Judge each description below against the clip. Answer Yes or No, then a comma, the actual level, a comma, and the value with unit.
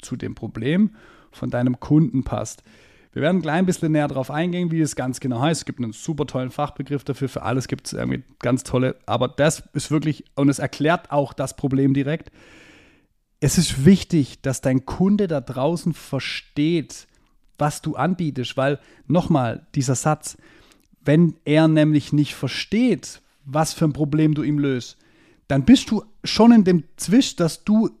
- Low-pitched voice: No, medium, 145 Hz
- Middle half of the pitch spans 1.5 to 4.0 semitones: Yes, average, 3.4 semitones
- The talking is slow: No, average, 175 wpm